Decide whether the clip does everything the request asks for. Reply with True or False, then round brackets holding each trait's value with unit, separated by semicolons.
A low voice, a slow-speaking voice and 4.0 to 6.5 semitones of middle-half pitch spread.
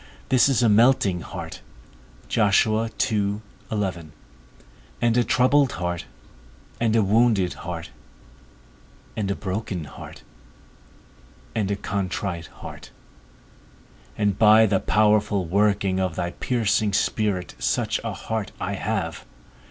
False (100 Hz; 105 wpm; 3.4 semitones)